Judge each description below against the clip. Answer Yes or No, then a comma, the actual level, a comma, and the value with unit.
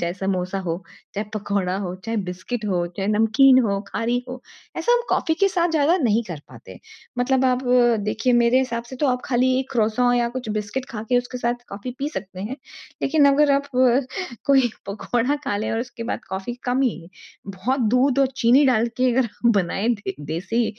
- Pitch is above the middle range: Yes, high, 240 Hz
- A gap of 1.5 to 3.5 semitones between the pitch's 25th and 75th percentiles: No, average, 4.3 semitones